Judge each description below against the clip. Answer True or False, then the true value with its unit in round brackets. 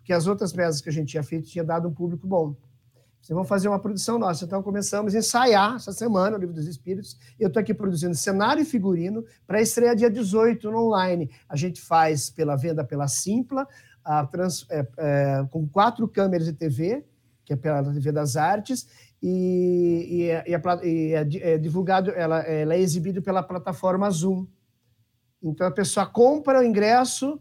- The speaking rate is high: True (195 wpm)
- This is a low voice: False (180 Hz)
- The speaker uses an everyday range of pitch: True (4.6 semitones)